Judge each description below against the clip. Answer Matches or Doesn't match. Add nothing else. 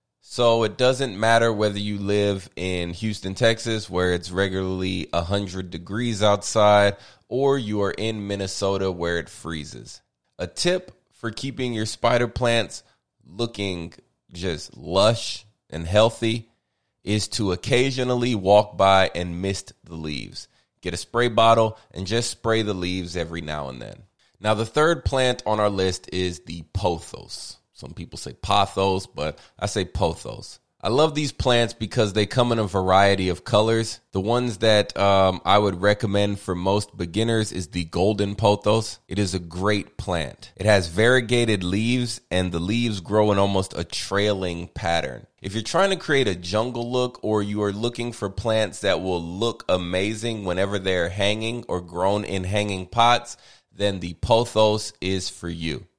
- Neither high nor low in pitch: Doesn't match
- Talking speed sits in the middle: Matches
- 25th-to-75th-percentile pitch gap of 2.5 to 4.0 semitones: Matches